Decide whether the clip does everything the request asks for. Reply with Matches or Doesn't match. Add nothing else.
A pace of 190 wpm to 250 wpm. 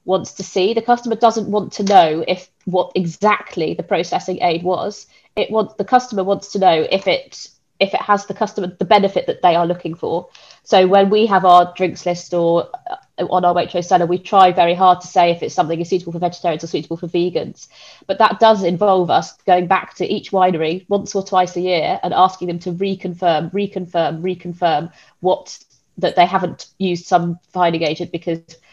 Matches